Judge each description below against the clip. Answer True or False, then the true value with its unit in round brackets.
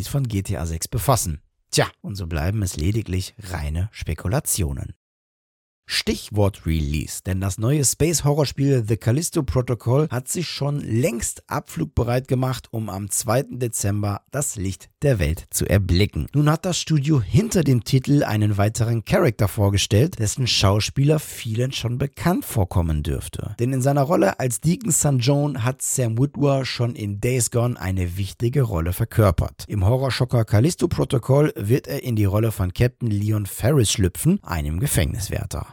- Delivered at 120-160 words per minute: True (150 wpm)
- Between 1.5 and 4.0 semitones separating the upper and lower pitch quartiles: False (5.6 semitones)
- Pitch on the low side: True (115 Hz)